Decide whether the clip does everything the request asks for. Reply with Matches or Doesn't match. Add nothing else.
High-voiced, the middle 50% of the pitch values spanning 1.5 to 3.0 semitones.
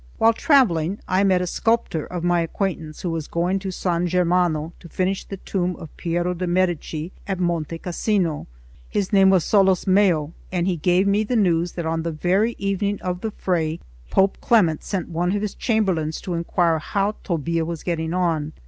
Doesn't match